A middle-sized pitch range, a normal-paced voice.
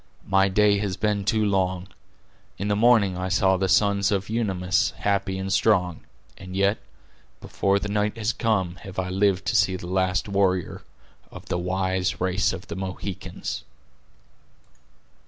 No: narrow, 1.5 semitones; average, 155 wpm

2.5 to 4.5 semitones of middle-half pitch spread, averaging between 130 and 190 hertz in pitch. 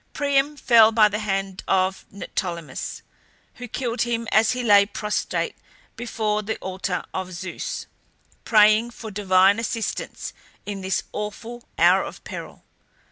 No: average, 3.2 semitones; high, 210 Hz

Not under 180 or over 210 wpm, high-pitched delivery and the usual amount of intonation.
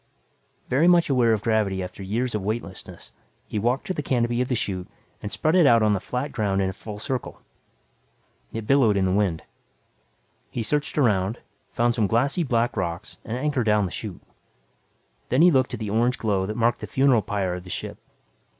No: average, 200 wpm; low, 115 Hz; average, 4.1 semitones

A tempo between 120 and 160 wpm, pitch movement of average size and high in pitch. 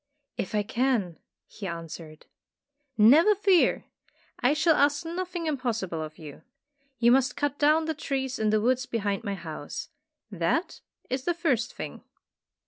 No: average, 150 wpm; wide, 7.1 semitones; very high, 250 Hz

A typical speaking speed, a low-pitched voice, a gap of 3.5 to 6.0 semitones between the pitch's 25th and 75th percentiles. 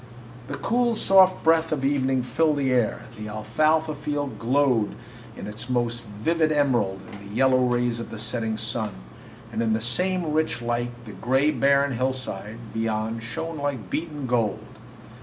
Yes: average, 160 wpm; low, 125 Hz; average, 4.6 semitones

